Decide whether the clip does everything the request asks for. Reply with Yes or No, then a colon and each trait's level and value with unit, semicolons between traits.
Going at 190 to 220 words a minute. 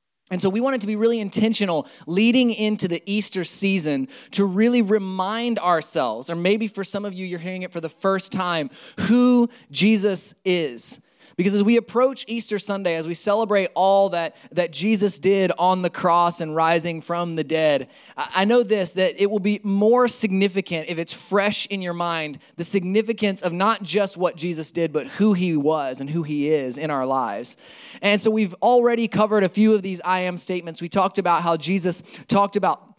Yes: average, 200 wpm